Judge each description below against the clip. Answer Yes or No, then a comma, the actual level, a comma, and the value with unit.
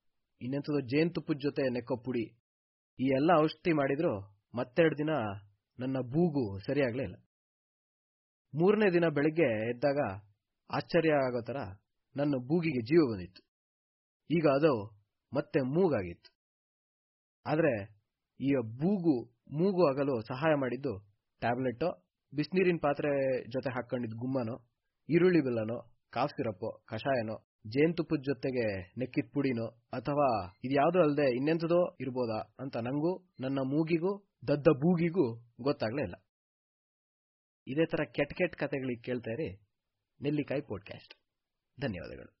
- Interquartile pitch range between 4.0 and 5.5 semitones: Yes, average, 5.0 semitones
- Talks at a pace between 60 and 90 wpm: No, fast, 105 wpm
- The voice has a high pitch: No, low, 135 Hz